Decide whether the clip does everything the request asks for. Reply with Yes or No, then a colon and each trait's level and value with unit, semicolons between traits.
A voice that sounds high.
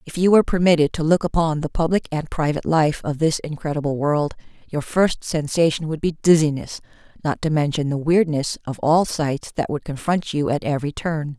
No: medium, 155 Hz